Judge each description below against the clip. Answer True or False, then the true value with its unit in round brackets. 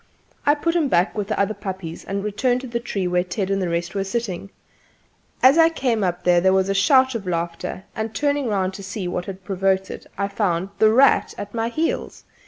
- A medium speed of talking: False (220 wpm)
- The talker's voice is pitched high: True (195 Hz)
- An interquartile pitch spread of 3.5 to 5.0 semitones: True (4.1 semitones)